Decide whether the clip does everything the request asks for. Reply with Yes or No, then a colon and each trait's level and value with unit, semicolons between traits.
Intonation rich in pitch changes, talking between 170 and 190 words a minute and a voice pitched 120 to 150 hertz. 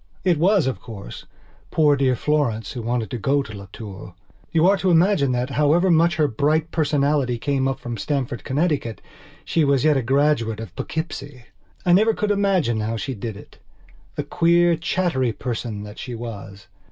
Yes: wide, 5.8 semitones; average, 175 wpm; medium, 140 Hz